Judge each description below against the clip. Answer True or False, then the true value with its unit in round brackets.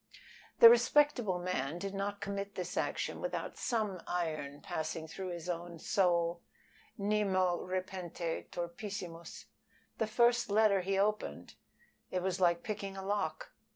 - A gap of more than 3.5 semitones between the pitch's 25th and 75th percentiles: False (3.0 semitones)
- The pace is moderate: False (130 wpm)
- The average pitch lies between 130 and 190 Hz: True (185 Hz)